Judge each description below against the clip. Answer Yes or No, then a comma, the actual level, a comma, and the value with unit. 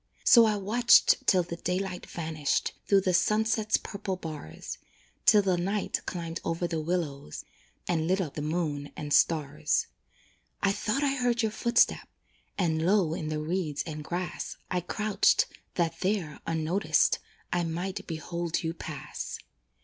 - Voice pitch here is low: No, medium, 175 Hz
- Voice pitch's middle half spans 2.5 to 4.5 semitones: Yes, average, 3.8 semitones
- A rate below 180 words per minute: Yes, average, 150 wpm